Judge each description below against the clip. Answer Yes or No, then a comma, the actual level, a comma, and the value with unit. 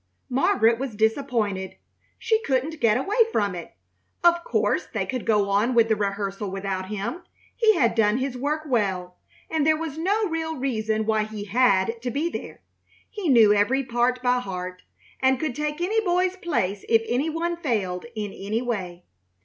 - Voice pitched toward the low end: No, high, 240 Hz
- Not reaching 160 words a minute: No, average, 175 wpm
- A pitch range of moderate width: No, wide, 6.9 semitones